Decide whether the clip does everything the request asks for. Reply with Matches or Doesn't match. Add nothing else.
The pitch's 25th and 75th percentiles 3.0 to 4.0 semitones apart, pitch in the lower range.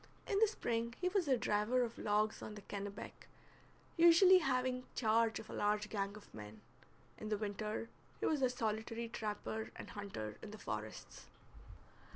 Doesn't match